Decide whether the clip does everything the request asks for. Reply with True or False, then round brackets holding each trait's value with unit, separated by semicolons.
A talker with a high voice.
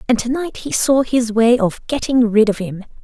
True (235 Hz)